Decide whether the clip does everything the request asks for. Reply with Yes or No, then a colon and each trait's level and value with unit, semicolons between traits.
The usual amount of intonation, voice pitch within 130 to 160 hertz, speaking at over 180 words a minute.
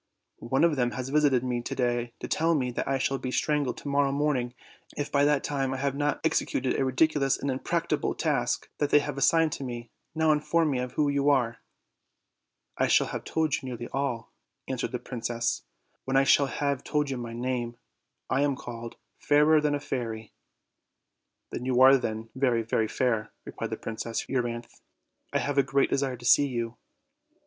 Yes: average, 3.0 semitones; low, 135 Hz; average, 190 wpm